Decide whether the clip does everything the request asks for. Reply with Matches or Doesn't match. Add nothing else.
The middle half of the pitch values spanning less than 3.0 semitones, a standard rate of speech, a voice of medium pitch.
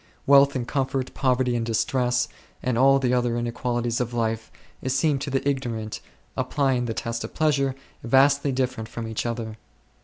Doesn't match